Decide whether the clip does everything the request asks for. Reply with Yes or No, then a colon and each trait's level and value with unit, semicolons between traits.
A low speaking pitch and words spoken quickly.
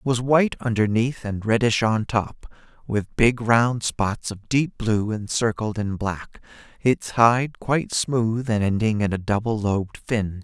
No: low, 110 Hz; average, 165 wpm